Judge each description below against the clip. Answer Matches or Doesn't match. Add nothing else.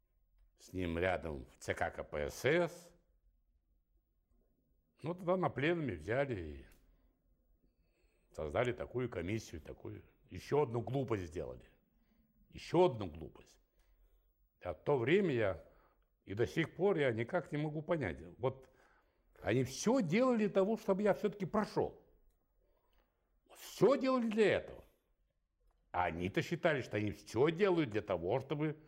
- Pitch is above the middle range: Doesn't match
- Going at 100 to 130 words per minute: Matches